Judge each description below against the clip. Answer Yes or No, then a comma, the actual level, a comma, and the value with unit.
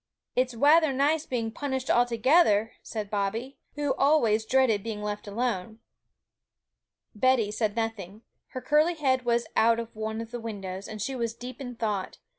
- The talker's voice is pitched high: Yes, high, 230 Hz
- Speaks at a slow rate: No, average, 165 wpm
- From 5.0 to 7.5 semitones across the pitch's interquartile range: No, average, 3.3 semitones